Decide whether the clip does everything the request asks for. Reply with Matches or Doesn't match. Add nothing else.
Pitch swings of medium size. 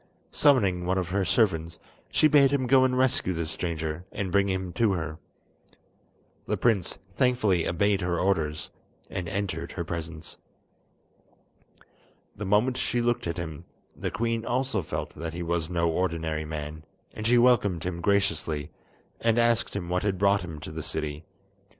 Matches